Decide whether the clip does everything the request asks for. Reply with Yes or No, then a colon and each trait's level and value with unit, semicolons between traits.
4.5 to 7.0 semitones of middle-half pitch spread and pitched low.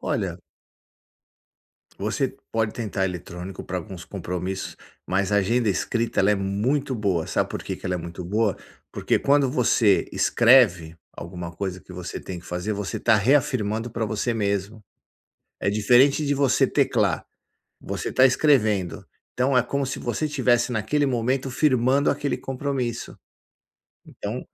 Yes: average, 5.1 semitones; low, 110 Hz